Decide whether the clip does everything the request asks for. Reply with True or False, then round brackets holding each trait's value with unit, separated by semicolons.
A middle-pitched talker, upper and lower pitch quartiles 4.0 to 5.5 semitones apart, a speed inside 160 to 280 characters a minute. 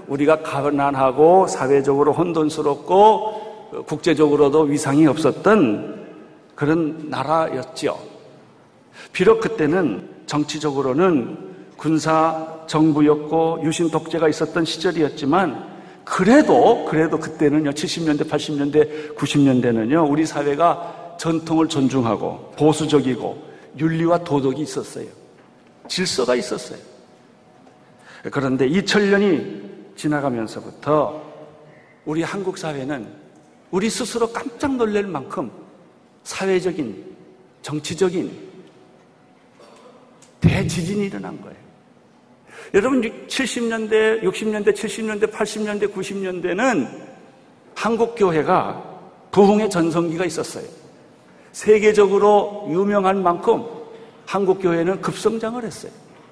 True (165 Hz; 5.1 semitones; 230 characters per minute)